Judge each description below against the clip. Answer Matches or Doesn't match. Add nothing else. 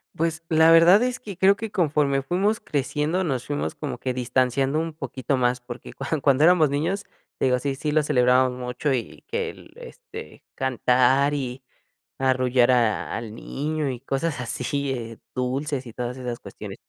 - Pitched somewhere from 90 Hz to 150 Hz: Matches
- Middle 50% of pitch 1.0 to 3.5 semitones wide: Doesn't match